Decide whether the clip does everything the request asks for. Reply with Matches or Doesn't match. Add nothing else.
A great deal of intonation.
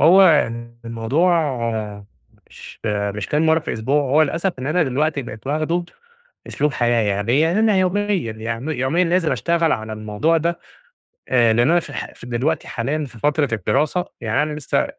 Matches